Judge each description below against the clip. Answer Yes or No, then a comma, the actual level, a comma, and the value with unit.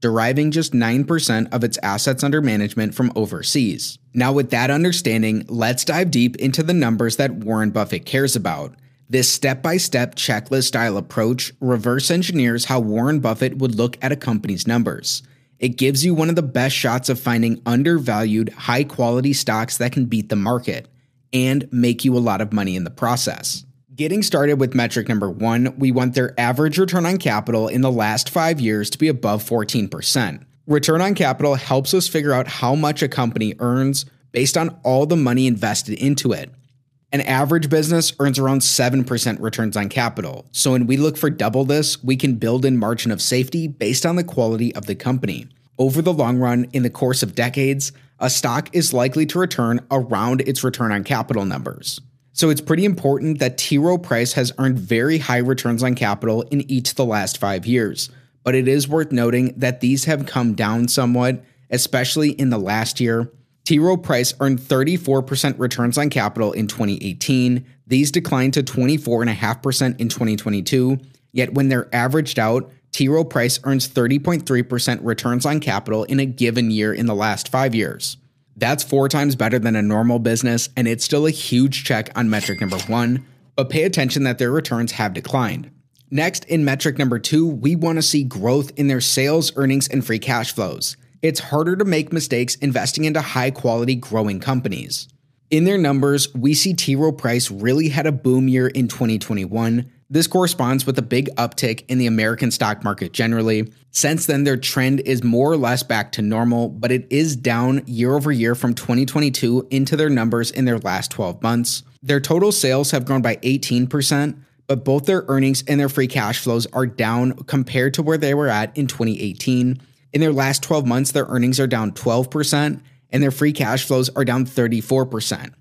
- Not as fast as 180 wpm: No, average, 185 wpm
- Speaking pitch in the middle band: No, low, 130 Hz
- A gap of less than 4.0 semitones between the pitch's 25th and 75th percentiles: Yes, average, 3.0 semitones